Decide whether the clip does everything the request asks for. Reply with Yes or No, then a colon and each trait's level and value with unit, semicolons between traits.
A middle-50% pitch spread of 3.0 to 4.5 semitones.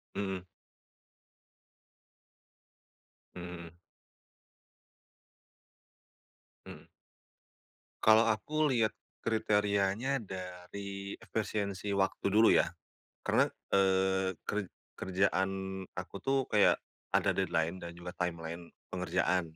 No: narrow, 2.4 semitones